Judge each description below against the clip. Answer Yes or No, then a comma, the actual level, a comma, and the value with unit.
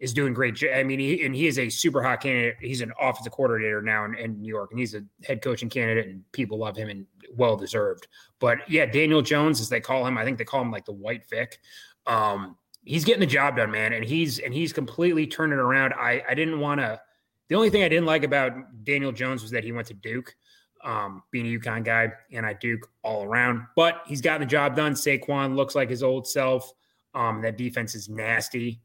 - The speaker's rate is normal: No, fast, 235 wpm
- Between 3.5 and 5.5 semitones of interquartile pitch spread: Yes, average, 4.0 semitones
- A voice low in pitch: Yes, low, 130 Hz